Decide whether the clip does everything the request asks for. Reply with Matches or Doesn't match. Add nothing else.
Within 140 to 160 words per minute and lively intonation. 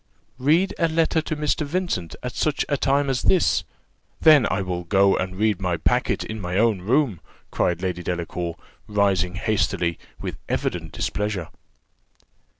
Matches